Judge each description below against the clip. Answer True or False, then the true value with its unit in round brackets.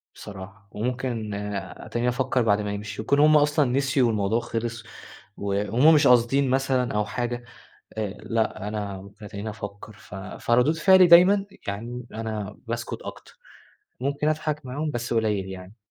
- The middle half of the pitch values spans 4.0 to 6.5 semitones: True (4.6 semitones)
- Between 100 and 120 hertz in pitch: True (115 Hz)